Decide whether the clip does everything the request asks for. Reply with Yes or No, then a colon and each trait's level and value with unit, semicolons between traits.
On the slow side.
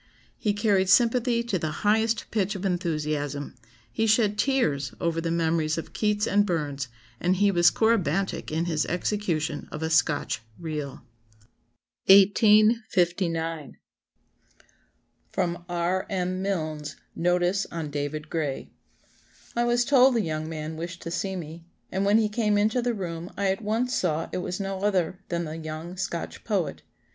No: average, 155 wpm